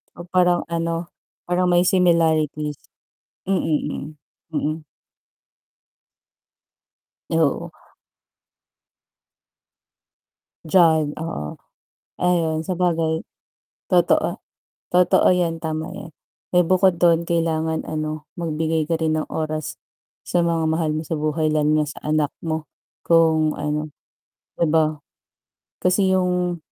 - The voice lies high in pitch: No, medium, 160 Hz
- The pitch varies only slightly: Yes, narrow, 1.9 semitones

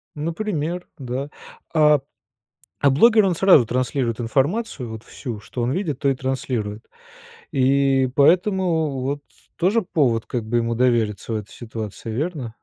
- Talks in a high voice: No, low, 135 Hz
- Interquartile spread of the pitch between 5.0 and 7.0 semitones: Yes, wide, 5.4 semitones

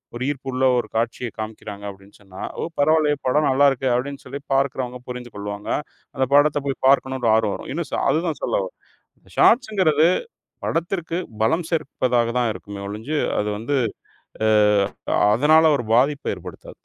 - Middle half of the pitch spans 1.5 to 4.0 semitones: No, average, 4.6 semitones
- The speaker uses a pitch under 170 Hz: Yes, low, 135 Hz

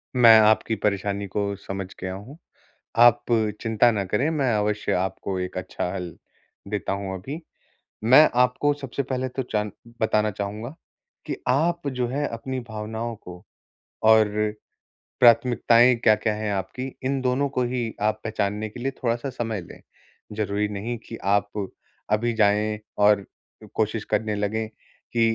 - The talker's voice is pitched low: Yes, low, 110 Hz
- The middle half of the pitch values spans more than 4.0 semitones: No, average, 3.1 semitones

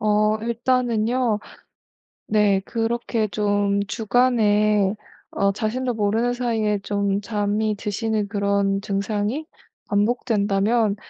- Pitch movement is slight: Yes, narrow, 2.2 semitones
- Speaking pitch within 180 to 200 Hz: No, high, 215 Hz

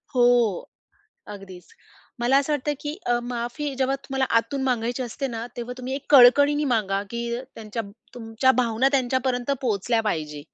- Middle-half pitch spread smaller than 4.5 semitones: Yes, average, 3.0 semitones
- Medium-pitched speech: No, high, 245 Hz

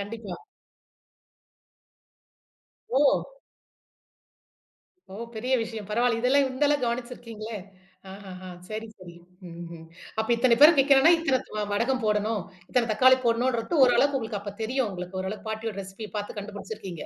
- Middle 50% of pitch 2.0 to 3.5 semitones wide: No, average, 3.9 semitones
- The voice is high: Yes, high, 225 Hz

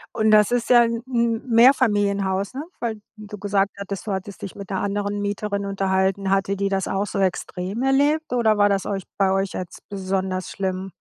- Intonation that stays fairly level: Yes, narrow, 2.2 semitones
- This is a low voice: No, high, 200 Hz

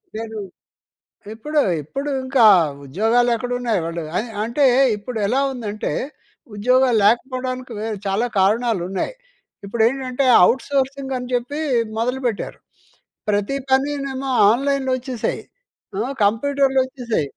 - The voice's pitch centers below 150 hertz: No, high, 245 Hz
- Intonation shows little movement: No, average, 3.3 semitones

